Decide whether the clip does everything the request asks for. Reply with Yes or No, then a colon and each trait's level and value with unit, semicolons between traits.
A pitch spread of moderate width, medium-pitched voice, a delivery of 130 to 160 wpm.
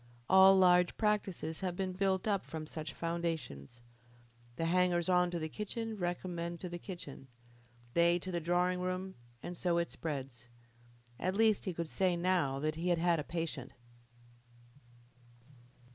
No: narrow, 2.1 semitones; medium, 175 Hz; average, 155 wpm